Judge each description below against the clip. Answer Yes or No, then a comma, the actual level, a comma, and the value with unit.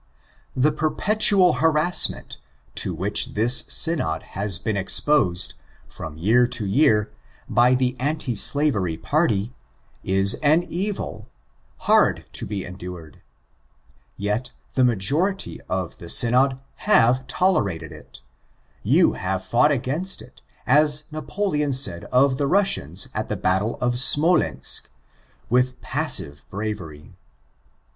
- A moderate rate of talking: No, slow, 115 wpm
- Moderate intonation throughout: No, wide, 7.8 semitones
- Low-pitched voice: Yes, low, 125 Hz